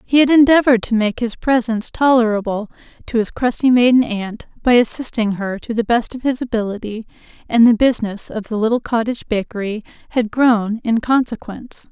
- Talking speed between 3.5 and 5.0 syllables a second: No, 5.6 syllables/s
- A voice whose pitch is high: Yes, high, 230 Hz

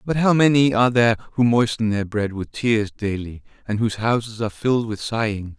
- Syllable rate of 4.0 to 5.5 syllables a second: No, 5.7 syllables/s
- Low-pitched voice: Yes, low, 110 Hz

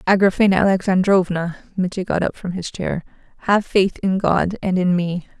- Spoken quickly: No, average, 165 wpm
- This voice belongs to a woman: Yes, female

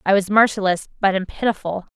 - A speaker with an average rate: Yes, average, 185 wpm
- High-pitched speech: Yes, high, 195 Hz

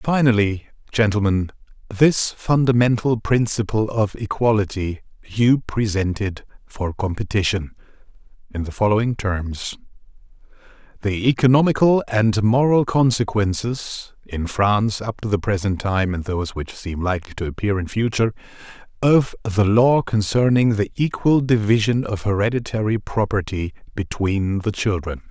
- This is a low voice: Yes, low, 105 Hz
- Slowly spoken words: Yes, slow, 115 wpm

